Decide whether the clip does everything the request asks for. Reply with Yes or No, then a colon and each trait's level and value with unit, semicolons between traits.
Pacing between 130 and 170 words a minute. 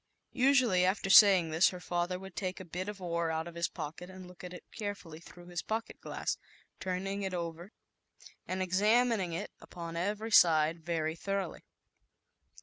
No: average, 185 wpm